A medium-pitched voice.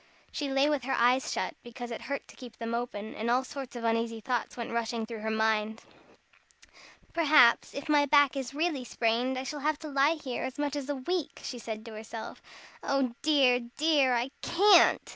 No: very high, 255 Hz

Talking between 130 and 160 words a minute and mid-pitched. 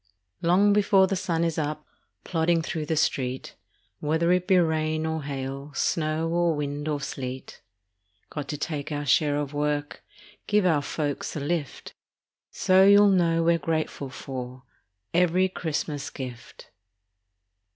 Yes: average, 140 wpm; medium, 155 Hz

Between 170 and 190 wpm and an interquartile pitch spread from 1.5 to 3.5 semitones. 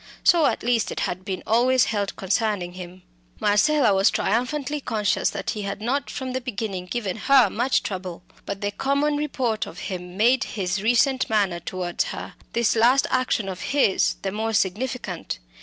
No: average, 175 wpm; average, 5.0 semitones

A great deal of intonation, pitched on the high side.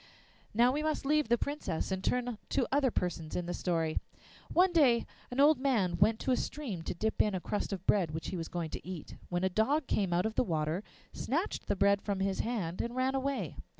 Yes: wide, 6.6 semitones; high, 210 Hz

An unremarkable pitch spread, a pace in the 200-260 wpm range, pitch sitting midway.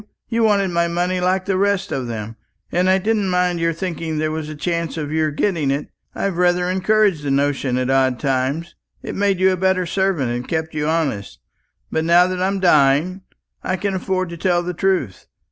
Yes: average, 3.8 semitones; fast, 205 wpm; medium, 175 Hz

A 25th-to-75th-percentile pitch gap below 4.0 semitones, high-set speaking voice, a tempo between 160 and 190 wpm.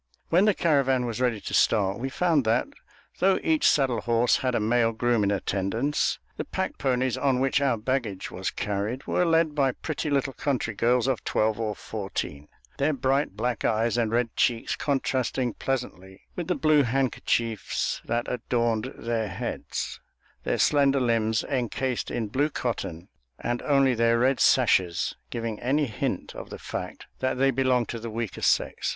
No: average, 3.3 semitones; low, 120 Hz; average, 170 wpm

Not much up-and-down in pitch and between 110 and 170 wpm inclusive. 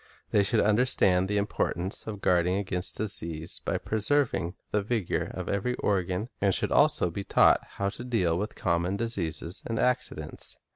No: average, 3.2 semitones; average, 160 wpm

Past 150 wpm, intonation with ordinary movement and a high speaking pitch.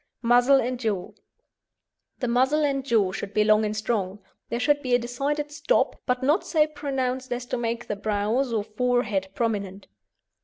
Yes: average, 175 wpm; average, 4.1 semitones; high, 245 Hz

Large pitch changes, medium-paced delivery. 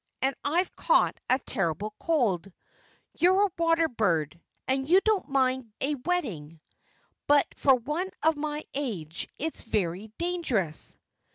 No: wide, 8.5 semitones; slow, 130 wpm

